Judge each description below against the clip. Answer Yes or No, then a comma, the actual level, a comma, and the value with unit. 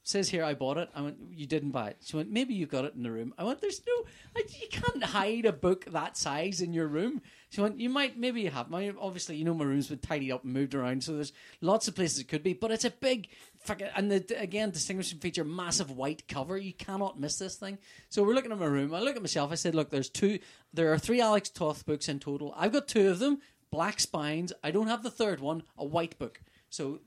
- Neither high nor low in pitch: Yes, medium, 180 Hz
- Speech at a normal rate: No, fast, 265 wpm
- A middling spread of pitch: No, wide, 6.0 semitones